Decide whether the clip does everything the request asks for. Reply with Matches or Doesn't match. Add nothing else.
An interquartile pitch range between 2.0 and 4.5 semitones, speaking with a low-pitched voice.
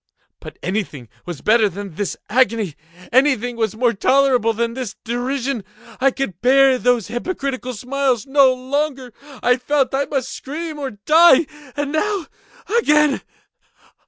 Doesn't match